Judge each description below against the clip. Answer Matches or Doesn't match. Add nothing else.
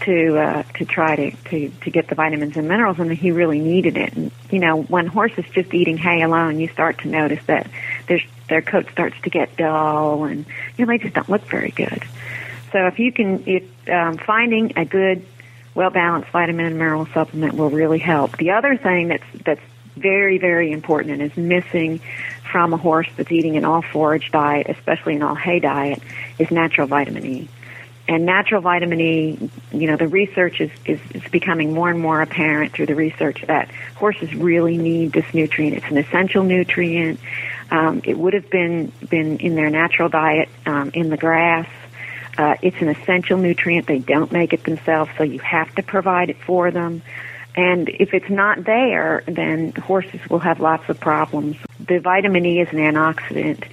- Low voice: Doesn't match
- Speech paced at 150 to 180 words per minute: Doesn't match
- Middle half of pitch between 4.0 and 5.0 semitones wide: Doesn't match